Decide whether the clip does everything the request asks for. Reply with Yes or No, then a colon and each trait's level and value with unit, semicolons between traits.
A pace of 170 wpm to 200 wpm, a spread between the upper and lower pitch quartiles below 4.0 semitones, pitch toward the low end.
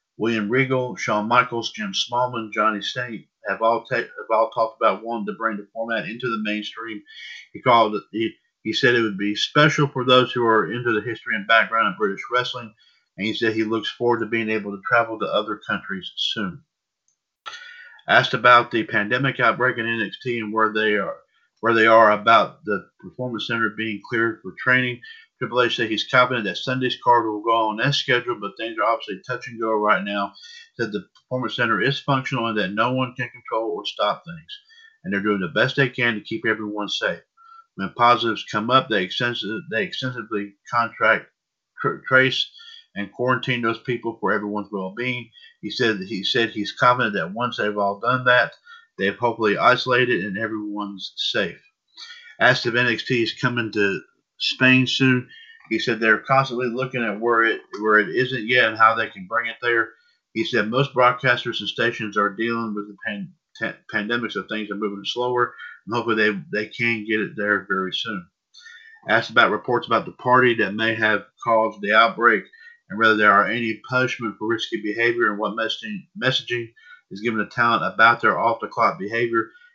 Yes: average, 190 wpm; average, 3.0 semitones; low, 120 Hz